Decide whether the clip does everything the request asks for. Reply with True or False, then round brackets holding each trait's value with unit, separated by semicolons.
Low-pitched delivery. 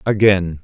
True (95 Hz)